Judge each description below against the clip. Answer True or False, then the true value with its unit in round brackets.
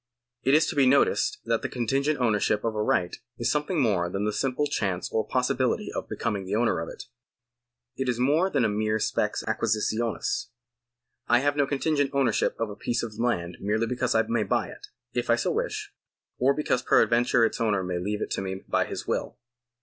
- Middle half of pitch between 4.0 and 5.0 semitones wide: True (4.6 semitones)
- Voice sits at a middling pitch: False (120 Hz)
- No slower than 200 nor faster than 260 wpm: True (205 wpm)